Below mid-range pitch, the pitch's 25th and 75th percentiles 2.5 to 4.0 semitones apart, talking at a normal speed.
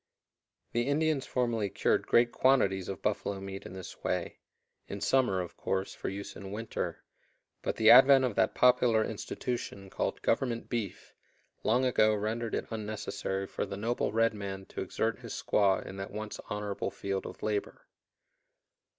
Yes: low, 110 Hz; average, 3.5 semitones; average, 160 wpm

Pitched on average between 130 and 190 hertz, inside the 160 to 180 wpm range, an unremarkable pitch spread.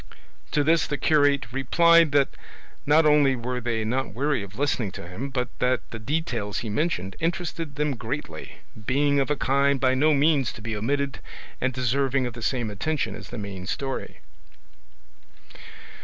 Yes: low, 135 Hz; average, 170 wpm; average, 3.7 semitones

